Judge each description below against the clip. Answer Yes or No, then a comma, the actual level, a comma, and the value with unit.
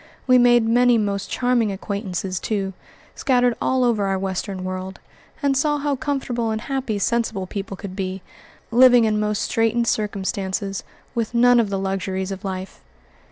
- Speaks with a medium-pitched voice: No, high, 215 Hz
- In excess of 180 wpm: No, average, 160 wpm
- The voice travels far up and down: No, average, 4.0 semitones